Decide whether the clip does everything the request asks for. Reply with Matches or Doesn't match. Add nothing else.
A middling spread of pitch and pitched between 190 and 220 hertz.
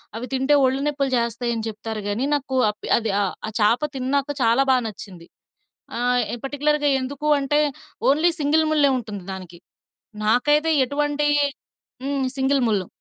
Doesn't match